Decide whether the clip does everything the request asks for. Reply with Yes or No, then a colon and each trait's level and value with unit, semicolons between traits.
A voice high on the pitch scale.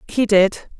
Yes: high, 210 Hz